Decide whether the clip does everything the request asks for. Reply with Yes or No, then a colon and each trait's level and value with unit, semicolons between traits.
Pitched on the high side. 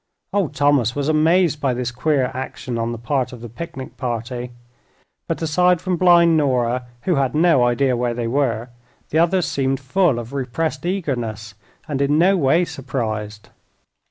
No: low, 135 Hz